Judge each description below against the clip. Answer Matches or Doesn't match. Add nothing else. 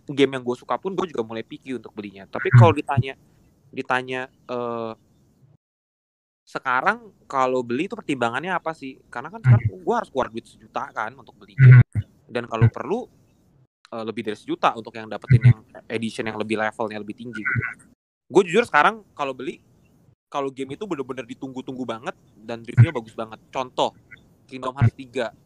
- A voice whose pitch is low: Matches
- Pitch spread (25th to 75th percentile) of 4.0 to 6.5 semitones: Doesn't match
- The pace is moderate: Doesn't match